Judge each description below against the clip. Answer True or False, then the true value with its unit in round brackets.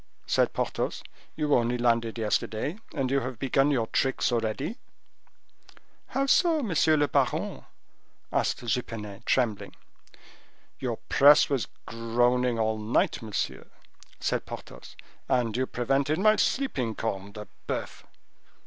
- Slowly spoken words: True (120 wpm)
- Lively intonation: False (3.8 semitones)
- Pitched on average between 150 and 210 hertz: False (125 Hz)